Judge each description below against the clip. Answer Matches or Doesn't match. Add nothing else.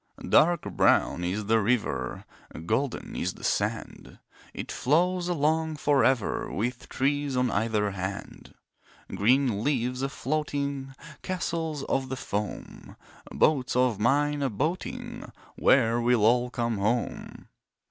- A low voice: Matches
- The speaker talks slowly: Matches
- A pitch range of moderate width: Matches